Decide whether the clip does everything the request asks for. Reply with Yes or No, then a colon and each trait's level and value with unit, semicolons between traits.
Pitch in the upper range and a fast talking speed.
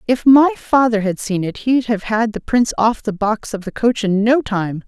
Yes: high, 225 Hz; fast, 245 wpm